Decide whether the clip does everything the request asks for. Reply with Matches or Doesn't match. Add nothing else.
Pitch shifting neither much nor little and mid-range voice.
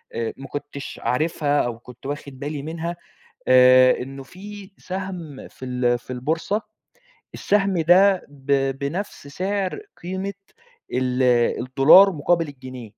Doesn't match